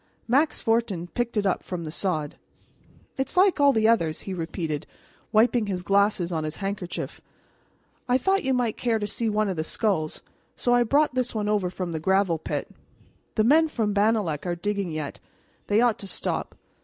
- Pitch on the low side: No, high, 205 Hz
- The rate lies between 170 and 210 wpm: Yes, average, 185 wpm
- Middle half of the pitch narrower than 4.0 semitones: No, average, 5.1 semitones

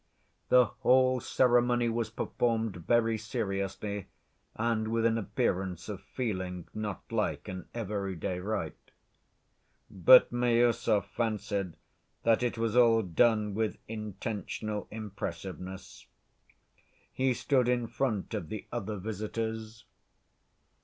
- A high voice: No, low, 110 Hz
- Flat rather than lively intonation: No, average, 3.1 semitones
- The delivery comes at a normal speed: No, slow, 105 wpm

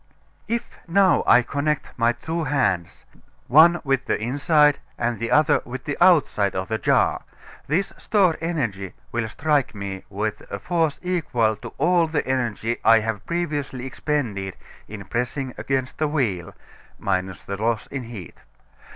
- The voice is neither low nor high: No, low, 130 Hz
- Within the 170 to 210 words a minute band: No, average, 150 wpm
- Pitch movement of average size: No, wide, 5.9 semitones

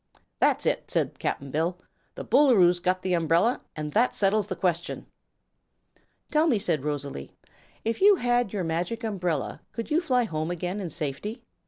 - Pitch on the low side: No, medium, 185 Hz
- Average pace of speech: Yes, average, 165 wpm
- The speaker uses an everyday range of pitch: No, wide, 5.8 semitones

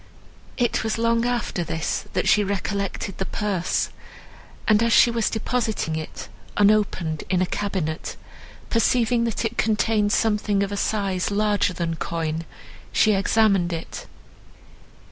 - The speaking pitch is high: Yes, high, 205 Hz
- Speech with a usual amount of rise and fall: Yes, average, 3.5 semitones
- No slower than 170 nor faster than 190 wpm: No, slow, 135 wpm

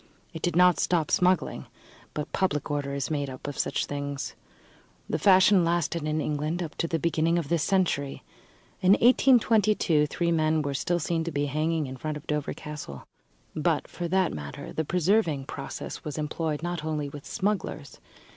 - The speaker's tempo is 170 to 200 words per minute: Yes, average, 175 wpm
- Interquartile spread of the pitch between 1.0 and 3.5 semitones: Yes, average, 3.1 semitones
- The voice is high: No, medium, 160 Hz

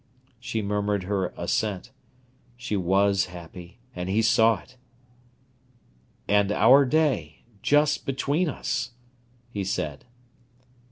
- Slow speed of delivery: Yes, slow, 100 wpm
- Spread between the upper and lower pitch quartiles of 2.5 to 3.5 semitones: No, average, 4.9 semitones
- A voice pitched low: Yes, low, 105 Hz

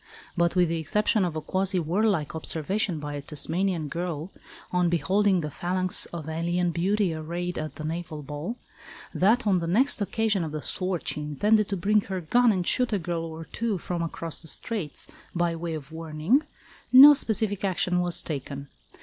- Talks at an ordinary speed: Yes, average, 185 wpm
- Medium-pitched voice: Yes, medium, 175 Hz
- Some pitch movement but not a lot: Yes, average, 3.8 semitones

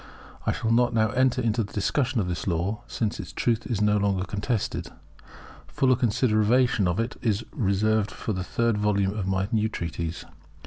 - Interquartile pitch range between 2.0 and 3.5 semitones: Yes, average, 3.1 semitones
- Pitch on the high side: No, low, 105 Hz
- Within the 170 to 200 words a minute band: Yes, average, 180 wpm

